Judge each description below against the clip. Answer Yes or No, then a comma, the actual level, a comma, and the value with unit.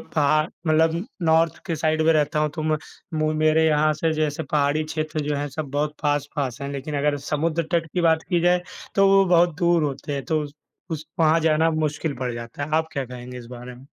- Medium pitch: Yes, medium, 155 Hz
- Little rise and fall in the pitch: Yes, narrow, 1.9 semitones